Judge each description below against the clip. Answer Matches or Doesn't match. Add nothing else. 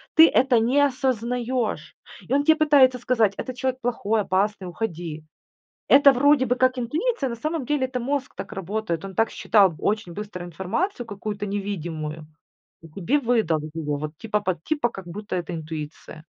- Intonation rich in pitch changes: Matches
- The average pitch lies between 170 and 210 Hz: Doesn't match